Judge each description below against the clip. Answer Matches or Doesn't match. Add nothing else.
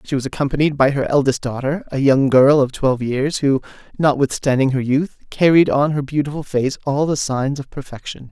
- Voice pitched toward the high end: Doesn't match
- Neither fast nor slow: Matches